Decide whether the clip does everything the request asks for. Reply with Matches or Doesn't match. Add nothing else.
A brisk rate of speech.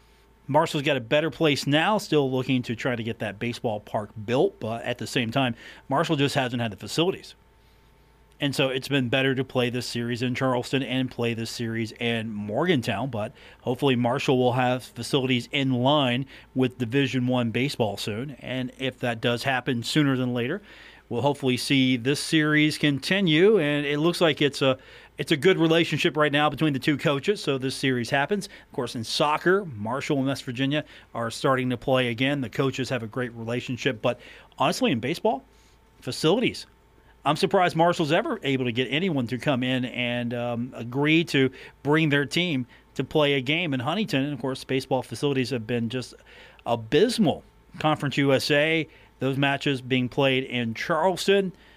Doesn't match